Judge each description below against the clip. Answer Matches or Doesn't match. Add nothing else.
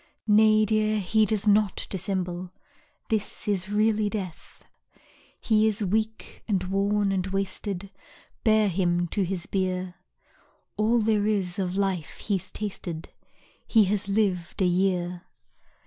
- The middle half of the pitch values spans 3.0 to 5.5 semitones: Doesn't match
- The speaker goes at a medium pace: Doesn't match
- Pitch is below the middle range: Doesn't match